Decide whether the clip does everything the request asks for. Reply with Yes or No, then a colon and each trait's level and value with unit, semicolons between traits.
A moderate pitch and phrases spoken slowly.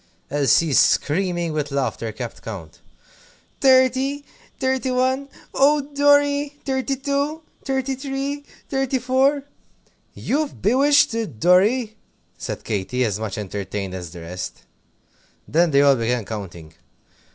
No: high, 230 Hz; slow, 120 wpm